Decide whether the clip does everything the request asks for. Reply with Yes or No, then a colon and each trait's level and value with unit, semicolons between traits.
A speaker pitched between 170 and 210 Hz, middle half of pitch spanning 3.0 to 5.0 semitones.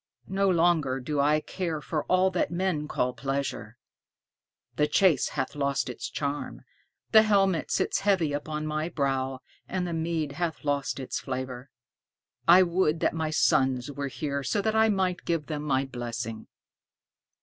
No: medium, 150 Hz; average, 4.4 semitones